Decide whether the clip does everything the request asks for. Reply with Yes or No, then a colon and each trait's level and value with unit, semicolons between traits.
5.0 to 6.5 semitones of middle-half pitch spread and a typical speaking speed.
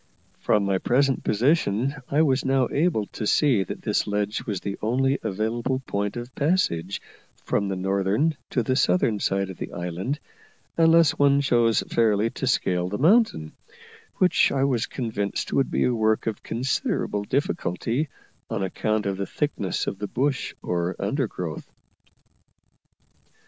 Yes: wide, 5.6 semitones; average, 150 wpm